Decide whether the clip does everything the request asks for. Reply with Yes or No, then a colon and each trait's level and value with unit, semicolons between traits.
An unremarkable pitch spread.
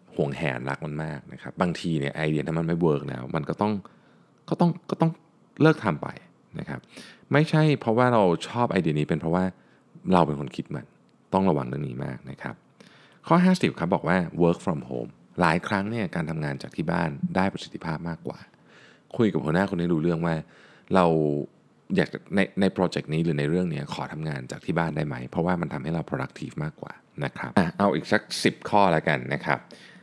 No: wide, 8.4 semitones